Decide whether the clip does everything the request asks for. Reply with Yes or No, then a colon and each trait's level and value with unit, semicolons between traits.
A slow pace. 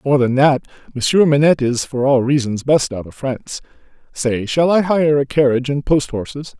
No: average, 200 wpm